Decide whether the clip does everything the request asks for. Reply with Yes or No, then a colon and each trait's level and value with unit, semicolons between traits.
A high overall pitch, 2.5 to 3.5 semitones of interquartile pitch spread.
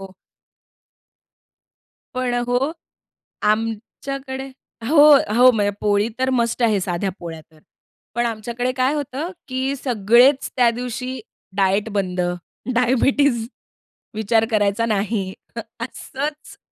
No: high, 235 Hz; average, 3.9 semitones